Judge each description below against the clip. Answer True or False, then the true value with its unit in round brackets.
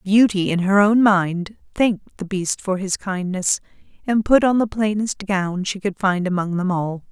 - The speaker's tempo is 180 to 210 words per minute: True (195 wpm)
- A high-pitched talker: True (195 Hz)